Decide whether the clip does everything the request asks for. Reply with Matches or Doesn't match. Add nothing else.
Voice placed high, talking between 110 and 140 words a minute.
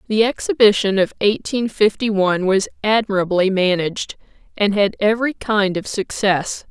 Matches